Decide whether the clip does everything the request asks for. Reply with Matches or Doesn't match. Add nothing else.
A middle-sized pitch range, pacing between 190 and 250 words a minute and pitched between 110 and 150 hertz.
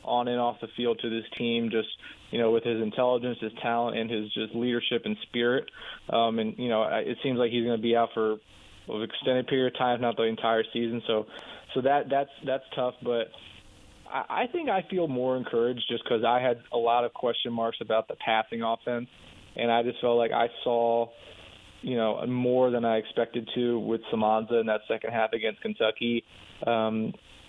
Doesn't match